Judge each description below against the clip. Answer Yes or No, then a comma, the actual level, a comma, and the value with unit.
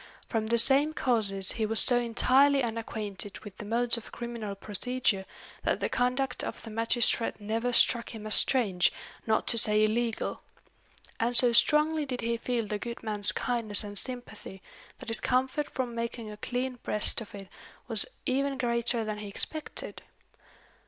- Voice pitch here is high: Yes, high, 230 Hz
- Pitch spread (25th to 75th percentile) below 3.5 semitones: Yes, narrow, 2.6 semitones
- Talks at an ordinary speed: Yes, average, 165 wpm